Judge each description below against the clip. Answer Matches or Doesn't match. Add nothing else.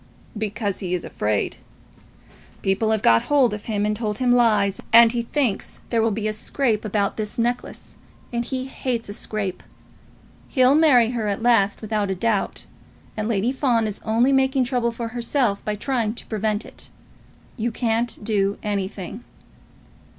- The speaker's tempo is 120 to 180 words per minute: Matches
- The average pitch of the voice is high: Matches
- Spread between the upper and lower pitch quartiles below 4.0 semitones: Matches